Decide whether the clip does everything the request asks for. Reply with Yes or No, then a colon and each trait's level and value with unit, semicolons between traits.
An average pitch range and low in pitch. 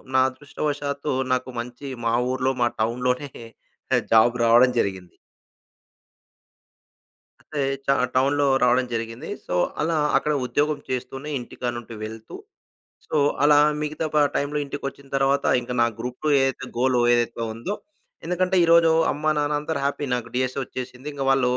Yes: average, 3.1 semitones; low, 130 Hz